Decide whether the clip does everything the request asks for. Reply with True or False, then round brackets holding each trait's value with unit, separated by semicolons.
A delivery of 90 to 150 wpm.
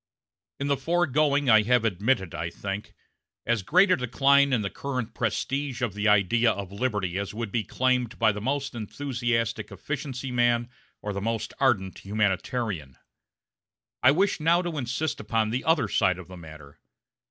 False (165 wpm)